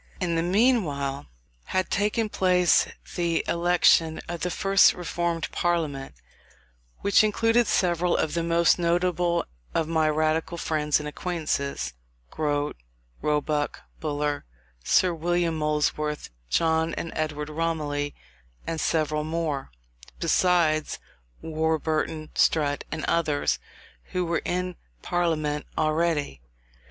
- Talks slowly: Yes, slow, 110 wpm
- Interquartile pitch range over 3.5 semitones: No, narrow, 2.4 semitones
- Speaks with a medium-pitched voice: Yes, medium, 160 Hz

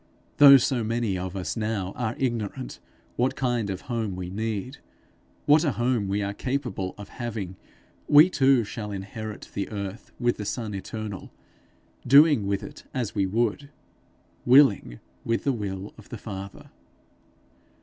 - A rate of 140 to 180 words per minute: Yes, average, 150 wpm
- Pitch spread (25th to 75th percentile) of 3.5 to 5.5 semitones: Yes, average, 4.0 semitones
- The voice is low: Yes, low, 110 Hz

